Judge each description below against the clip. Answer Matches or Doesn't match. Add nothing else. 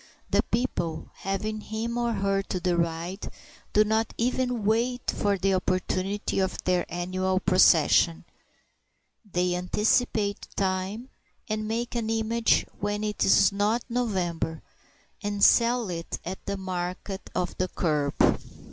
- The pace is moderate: Doesn't match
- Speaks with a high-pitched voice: Matches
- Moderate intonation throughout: Matches